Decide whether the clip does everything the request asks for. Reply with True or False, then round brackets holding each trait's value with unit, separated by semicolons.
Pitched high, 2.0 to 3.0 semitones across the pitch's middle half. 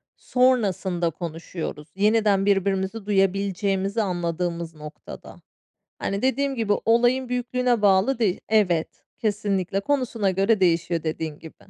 False (195 Hz; 4.3 semitones)